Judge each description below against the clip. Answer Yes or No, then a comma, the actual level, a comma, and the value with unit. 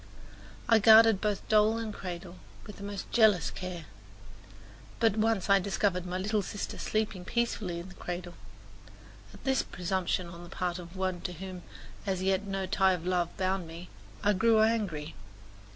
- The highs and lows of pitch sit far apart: No, average, 3.1 semitones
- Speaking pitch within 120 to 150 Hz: No, high, 190 Hz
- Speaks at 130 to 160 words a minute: No, average, 170 wpm